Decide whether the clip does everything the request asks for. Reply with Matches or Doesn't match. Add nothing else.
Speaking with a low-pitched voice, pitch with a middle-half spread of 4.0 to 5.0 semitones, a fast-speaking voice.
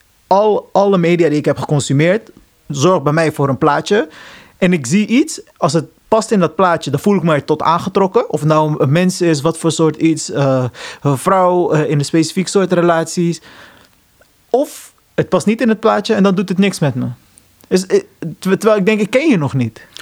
Doesn't match